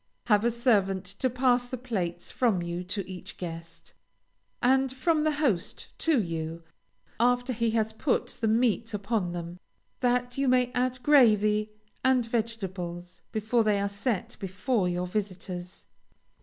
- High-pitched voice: Yes, high, 220 Hz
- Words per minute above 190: No, average, 145 wpm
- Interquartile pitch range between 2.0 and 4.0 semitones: No, average, 5.1 semitones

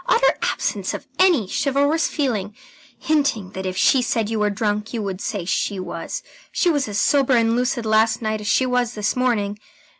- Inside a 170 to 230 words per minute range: Yes, average, 190 wpm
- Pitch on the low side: No, high, 225 Hz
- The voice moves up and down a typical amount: Yes, average, 4.1 semitones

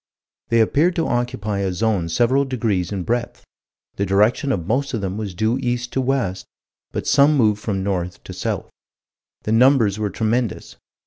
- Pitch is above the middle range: No, low, 110 Hz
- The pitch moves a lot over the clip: No, average, 4.3 semitones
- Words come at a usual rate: Yes, average, 175 wpm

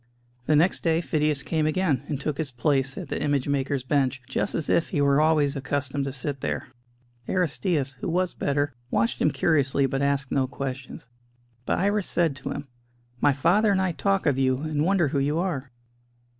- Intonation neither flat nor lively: Yes, average, 3.0 semitones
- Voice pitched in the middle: Yes, medium, 145 Hz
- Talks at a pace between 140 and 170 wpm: No, average, 195 wpm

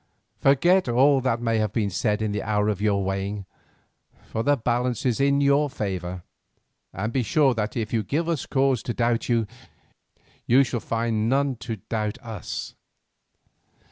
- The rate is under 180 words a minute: Yes, average, 170 wpm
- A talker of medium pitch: No, low, 115 Hz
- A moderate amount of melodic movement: Yes, average, 4.0 semitones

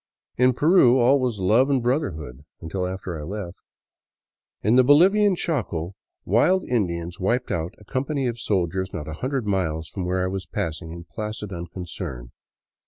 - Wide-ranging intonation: Yes, wide, 6.8 semitones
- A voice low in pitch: Yes, low, 100 Hz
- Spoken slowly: No, average, 170 wpm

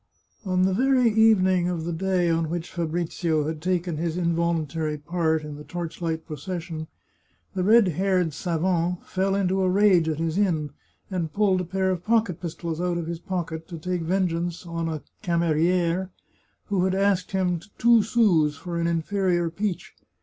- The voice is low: No, medium, 175 Hz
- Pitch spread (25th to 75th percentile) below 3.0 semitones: Yes, narrow, 2.4 semitones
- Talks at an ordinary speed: Yes, average, 170 wpm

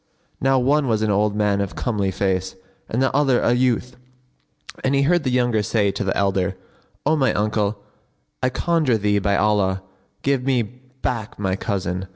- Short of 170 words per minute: No, average, 180 wpm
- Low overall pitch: Yes, low, 110 Hz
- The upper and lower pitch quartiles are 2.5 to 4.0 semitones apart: No, average, 4.4 semitones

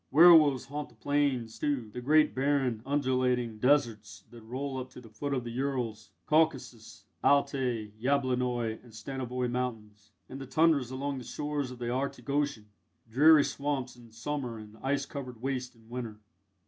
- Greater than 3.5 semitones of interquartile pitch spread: No, average, 3.2 semitones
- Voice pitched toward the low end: Yes, low, 125 Hz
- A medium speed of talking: Yes, average, 160 wpm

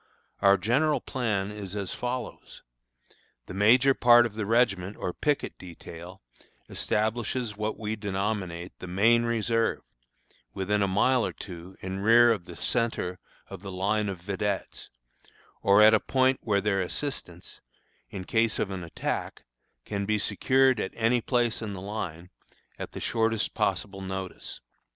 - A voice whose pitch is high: No, low, 105 Hz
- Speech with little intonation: No, average, 3.3 semitones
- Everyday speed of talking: Yes, average, 150 wpm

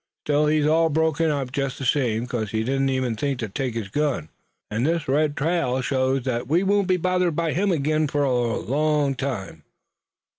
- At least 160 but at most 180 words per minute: No, average, 195 wpm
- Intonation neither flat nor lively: Yes, average, 3.8 semitones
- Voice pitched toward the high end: No, medium, 140 Hz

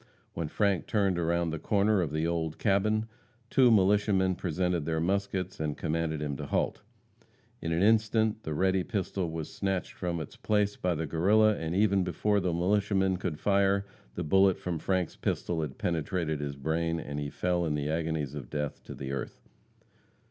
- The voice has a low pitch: Yes, very low, 90 Hz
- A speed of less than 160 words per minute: No, average, 180 wpm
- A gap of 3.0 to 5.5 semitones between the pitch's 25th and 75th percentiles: Yes, average, 3.7 semitones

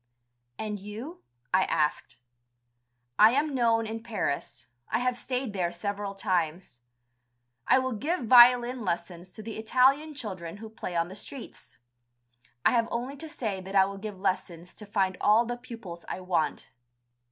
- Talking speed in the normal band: Yes, average, 160 wpm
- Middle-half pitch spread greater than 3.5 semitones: Yes, average, 4.7 semitones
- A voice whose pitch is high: Yes, high, 215 Hz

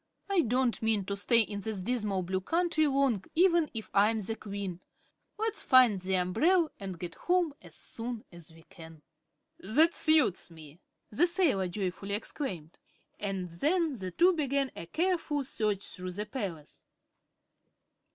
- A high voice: Yes, high, 215 Hz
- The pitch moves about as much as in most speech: No, wide, 8.0 semitones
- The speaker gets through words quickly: No, average, 155 wpm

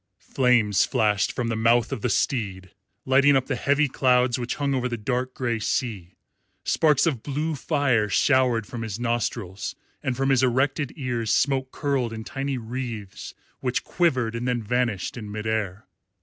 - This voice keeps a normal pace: Yes, average, 170 wpm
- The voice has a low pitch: Yes, low, 125 Hz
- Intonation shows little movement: No, average, 3.1 semitones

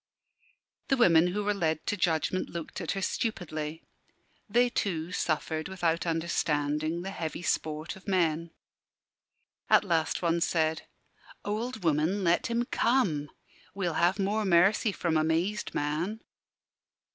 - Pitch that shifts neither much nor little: Yes, average, 3.9 semitones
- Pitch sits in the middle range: Yes, medium, 170 Hz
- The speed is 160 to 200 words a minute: No, slow, 135 wpm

